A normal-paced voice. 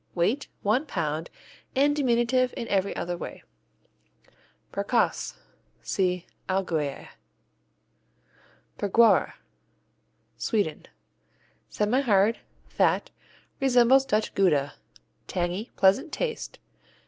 No: slow, 75 wpm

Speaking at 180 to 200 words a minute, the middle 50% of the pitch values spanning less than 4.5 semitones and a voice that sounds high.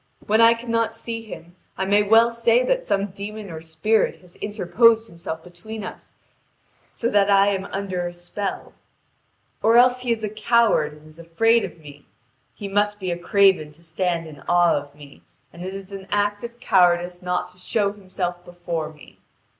Yes: average, 185 wpm; average, 4.0 semitones; high, 195 Hz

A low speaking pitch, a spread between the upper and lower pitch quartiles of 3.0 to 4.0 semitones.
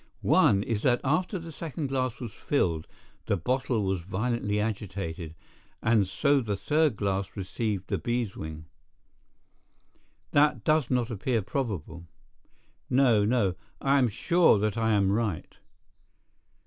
No: low, 110 Hz; average, 4.9 semitones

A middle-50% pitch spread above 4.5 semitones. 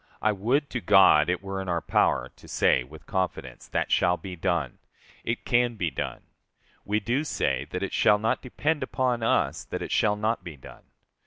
Yes: average, 5.2 semitones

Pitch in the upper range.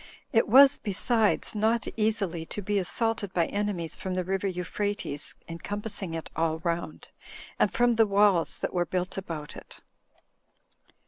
Yes: high, 195 Hz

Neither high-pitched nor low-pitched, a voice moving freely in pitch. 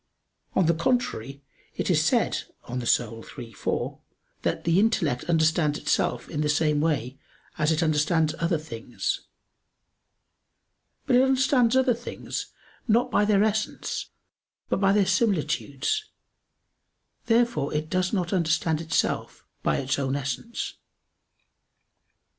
Yes: medium, 165 Hz; wide, 6.3 semitones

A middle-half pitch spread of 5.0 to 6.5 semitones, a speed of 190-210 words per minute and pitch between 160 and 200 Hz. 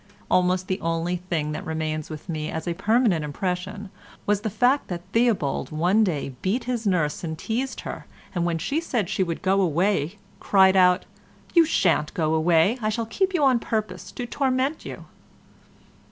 No: wide, 5.4 semitones; average, 170 wpm; medium, 185 Hz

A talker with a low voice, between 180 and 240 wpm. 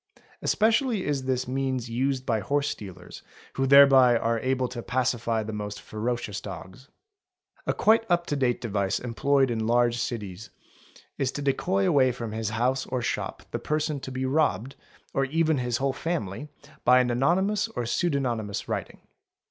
No: low, 130 Hz; average, 170 wpm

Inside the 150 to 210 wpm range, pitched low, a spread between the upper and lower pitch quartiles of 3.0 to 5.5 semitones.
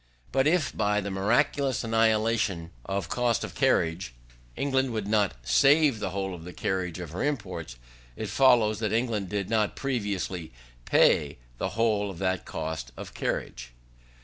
Yes: average, 155 wpm; low, 105 Hz; average, 4.5 semitones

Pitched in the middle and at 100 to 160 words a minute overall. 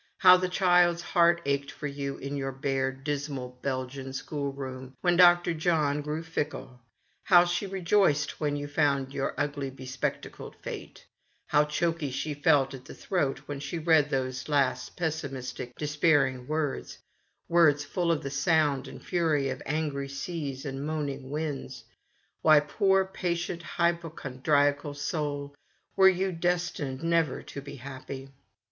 Yes: medium, 145 Hz; average, 150 wpm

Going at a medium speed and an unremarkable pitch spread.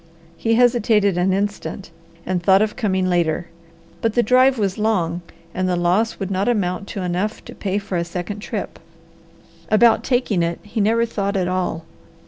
Yes: average, 175 wpm; average, 3.4 semitones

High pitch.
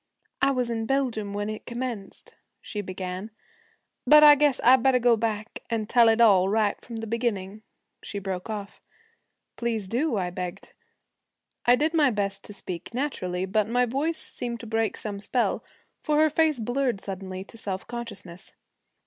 Yes: high, 225 Hz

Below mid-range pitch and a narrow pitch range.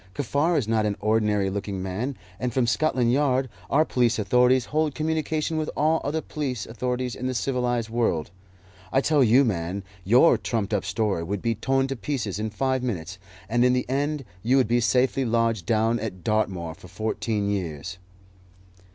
No: low, 120 Hz; average, 4.2 semitones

